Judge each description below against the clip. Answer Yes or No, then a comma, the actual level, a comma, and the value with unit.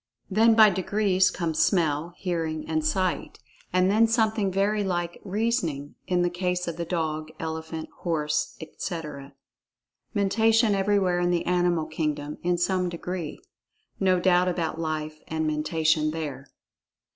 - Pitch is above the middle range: No, medium, 175 Hz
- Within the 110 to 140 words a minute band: Yes, slow, 135 wpm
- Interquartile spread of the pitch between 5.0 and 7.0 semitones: No, average, 3.3 semitones